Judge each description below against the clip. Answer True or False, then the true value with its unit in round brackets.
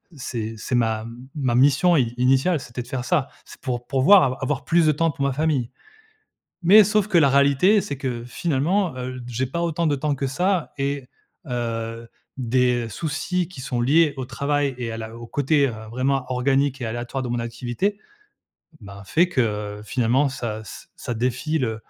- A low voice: True (130 Hz)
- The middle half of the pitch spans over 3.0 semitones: True (3.8 semitones)